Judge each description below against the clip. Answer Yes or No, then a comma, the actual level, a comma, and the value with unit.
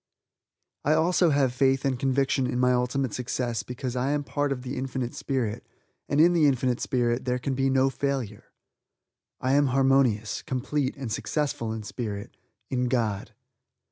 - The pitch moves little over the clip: Yes, narrow, 2.0 semitones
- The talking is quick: No, average, 170 wpm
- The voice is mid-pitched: No, low, 130 Hz